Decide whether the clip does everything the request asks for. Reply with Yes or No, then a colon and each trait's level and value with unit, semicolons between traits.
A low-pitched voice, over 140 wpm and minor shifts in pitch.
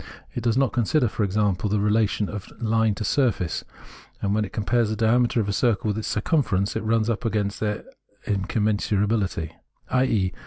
Yes: low, 110 Hz; average, 180 wpm; narrow, 2.2 semitones